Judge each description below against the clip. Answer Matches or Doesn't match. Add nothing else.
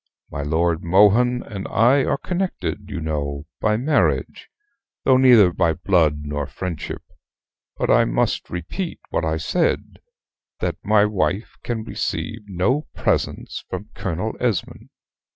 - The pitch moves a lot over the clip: Matches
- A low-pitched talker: Matches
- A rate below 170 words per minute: Matches